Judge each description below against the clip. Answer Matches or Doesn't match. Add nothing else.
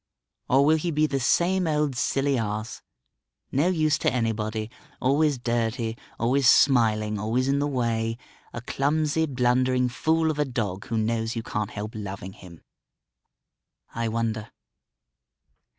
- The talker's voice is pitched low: Matches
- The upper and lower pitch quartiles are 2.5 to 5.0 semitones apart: Matches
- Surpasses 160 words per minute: Doesn't match